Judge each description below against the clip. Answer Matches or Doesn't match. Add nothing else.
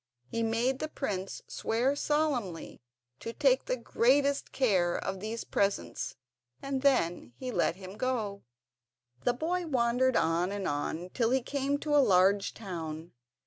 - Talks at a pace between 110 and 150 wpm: Matches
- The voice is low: Doesn't match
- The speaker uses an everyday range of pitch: Doesn't match